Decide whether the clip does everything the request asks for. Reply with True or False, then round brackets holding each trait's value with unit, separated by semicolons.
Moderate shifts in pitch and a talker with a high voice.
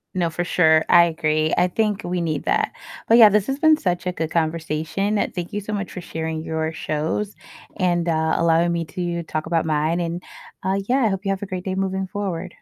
False (3.1 semitones; 175 Hz)